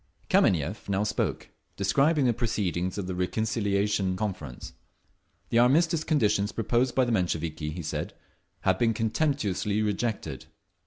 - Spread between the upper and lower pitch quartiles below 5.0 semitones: Yes, average, 4.4 semitones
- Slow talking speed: Yes, slow, 125 wpm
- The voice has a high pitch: No, low, 105 Hz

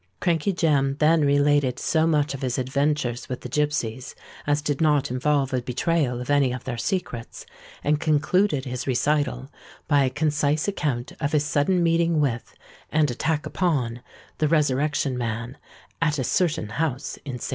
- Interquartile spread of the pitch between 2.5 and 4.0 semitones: Yes, average, 3.1 semitones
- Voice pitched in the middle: Yes, medium, 145 Hz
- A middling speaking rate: Yes, average, 170 wpm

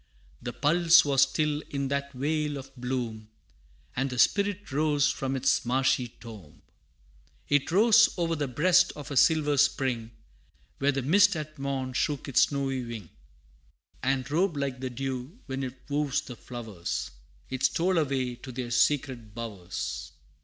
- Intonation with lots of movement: No, average, 3.0 semitones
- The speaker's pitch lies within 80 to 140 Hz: Yes, low, 135 Hz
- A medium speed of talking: Yes, average, 155 wpm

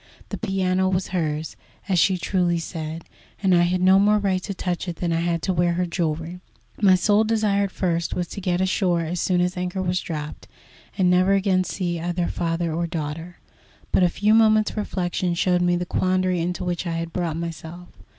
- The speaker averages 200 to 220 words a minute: Yes, fast, 205 wpm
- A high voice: No, medium, 180 Hz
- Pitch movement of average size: No, narrow, 1.8 semitones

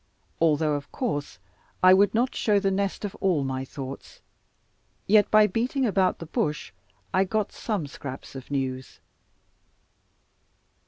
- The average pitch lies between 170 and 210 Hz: Yes, medium, 185 Hz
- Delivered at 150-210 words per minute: No, average, 140 wpm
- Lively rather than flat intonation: Yes, wide, 6.5 semitones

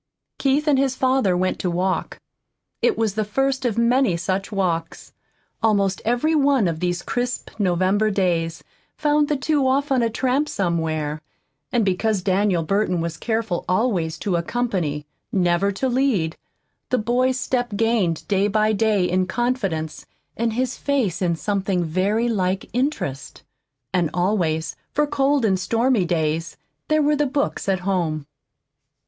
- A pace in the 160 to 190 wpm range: No, average, 150 wpm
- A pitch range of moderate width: No, wide, 6.0 semitones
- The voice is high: Yes, high, 205 Hz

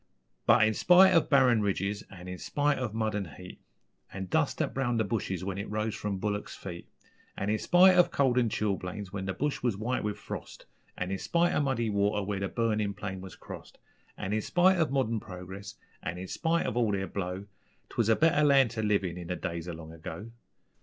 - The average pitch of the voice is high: No, low, 105 Hz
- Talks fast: Yes, fast, 220 wpm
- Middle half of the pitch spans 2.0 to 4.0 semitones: No, average, 4.4 semitones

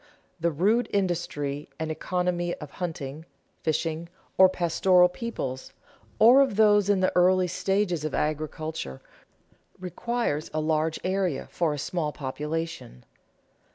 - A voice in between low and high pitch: Yes, medium, 170 Hz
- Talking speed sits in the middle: No, slow, 120 wpm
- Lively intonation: No, average, 3.4 semitones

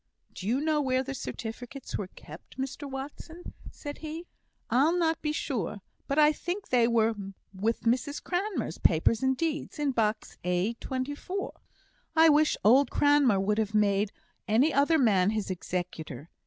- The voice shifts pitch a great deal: Yes, wide, 6.0 semitones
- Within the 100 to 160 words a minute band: Yes, average, 155 wpm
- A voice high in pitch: Yes, very high, 260 Hz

